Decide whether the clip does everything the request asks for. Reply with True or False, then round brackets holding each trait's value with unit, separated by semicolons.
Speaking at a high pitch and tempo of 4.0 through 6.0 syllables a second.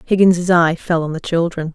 False (170 Hz; 5.0 syllables/s)